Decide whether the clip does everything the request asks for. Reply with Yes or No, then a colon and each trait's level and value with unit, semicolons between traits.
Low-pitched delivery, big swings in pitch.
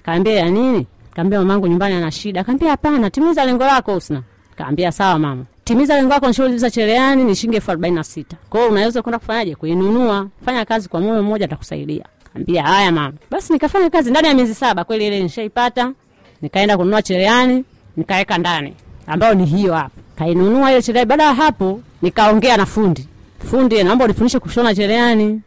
No: high, 210 Hz; wide, 5.9 semitones